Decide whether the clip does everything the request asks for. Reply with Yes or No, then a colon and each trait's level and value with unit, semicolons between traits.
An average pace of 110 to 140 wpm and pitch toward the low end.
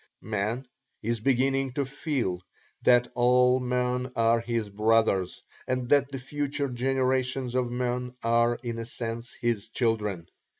Yes: slow, 135 wpm; low, 125 Hz